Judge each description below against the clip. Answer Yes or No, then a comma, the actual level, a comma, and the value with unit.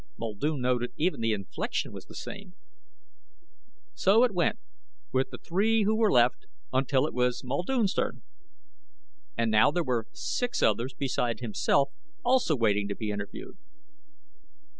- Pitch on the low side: Yes, low, 130 Hz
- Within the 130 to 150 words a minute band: Yes, average, 140 wpm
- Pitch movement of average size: No, wide, 8.0 semitones